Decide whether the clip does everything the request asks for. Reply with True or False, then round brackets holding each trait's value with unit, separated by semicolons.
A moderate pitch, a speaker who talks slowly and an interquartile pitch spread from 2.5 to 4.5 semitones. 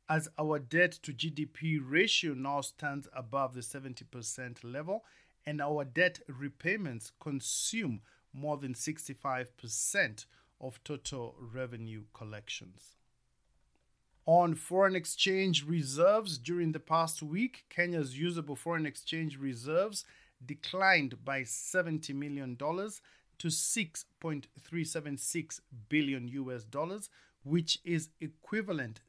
True (150 Hz; 105 wpm; 4.2 semitones)